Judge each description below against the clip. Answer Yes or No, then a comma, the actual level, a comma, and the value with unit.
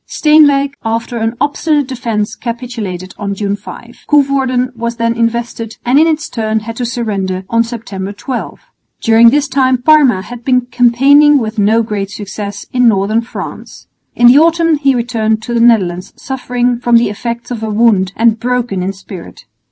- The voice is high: Yes, high, 235 Hz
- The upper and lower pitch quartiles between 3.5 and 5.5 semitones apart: No, average, 2.8 semitones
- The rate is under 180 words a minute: Yes, average, 170 wpm